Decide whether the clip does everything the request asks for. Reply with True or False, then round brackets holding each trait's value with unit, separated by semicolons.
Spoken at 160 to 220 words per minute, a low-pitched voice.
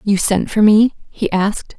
False (200 wpm; 205 Hz)